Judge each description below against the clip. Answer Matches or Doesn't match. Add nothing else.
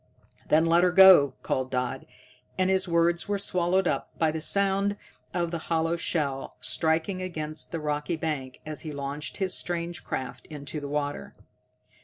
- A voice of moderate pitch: Matches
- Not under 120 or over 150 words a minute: Doesn't match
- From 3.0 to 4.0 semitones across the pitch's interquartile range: Matches